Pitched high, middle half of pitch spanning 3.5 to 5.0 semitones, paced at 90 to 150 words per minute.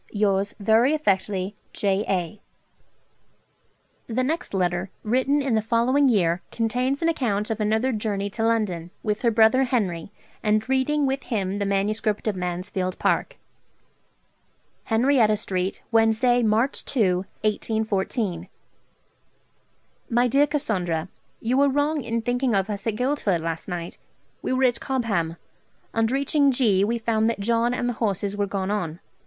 Yes: high, 220 Hz; average, 4.1 semitones; average, 145 wpm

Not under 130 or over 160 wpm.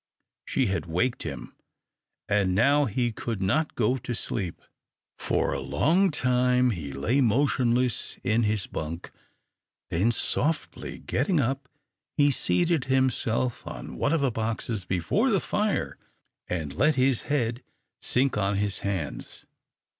Yes: slow, 135 wpm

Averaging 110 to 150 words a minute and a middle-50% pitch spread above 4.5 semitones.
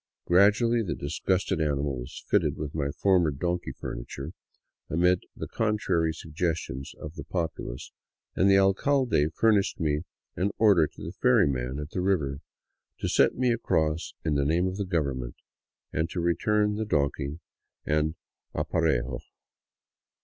Yes: average, 145 wpm; average, 4.9 semitones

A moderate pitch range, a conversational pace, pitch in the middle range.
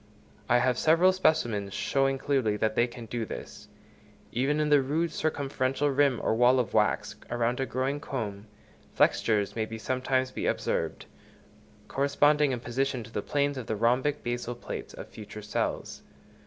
No: average, 3.6 semitones; average, 160 wpm; low, 130 Hz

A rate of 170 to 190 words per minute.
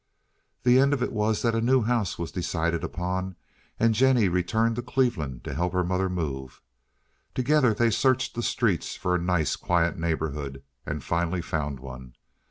Yes: average, 175 wpm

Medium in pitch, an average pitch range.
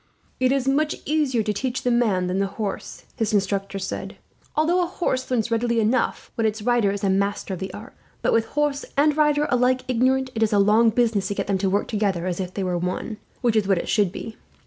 No: high, 225 Hz; average, 4.5 semitones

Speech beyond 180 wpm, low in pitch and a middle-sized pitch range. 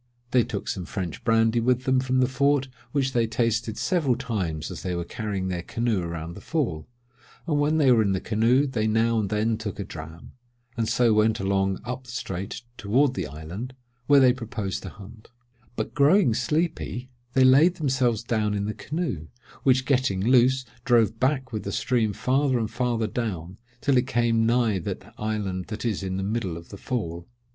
Yes: average, 195 wpm; low, 115 Hz; average, 4.5 semitones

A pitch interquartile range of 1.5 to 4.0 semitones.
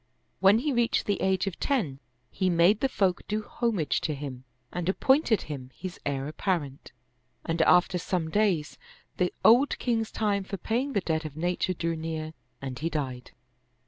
No: average, 5.2 semitones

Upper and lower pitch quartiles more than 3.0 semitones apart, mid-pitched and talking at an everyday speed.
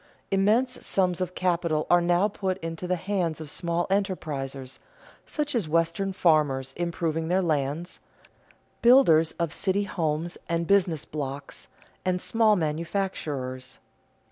No: average, 3.6 semitones; medium, 170 Hz; slow, 125 wpm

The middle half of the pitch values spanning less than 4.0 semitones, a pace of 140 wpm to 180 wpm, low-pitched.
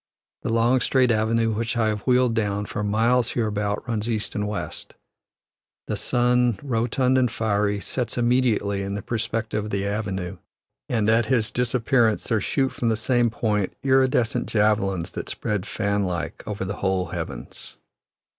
Yes: average, 2.8 semitones; average, 160 wpm; low, 110 Hz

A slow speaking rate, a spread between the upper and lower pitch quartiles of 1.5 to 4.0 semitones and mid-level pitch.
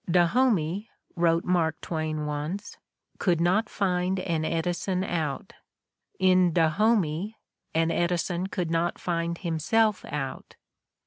Yes: slow, 110 wpm; narrow, 2.4 semitones; medium, 175 Hz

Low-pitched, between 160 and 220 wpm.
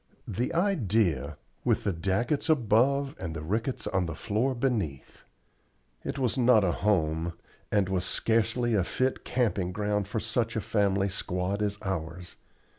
No: low, 105 Hz; average, 150 wpm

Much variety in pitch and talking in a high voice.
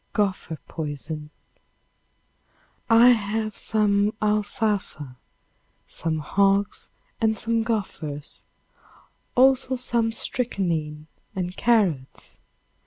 Yes: wide, 5.9 semitones; high, 205 Hz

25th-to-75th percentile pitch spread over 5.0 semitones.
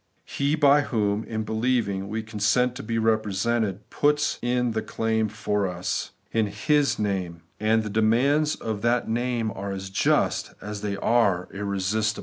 No: average, 2.8 semitones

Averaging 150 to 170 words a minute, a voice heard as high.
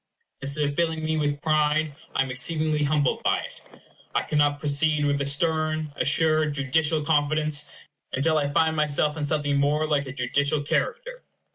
No: average, 165 wpm; medium, 150 Hz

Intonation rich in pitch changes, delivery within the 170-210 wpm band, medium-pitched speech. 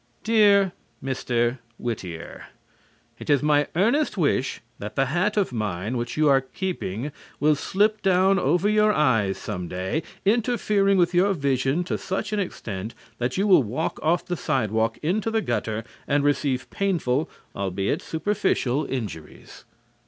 No: wide, 8.4 semitones; average, 145 wpm; medium, 150 Hz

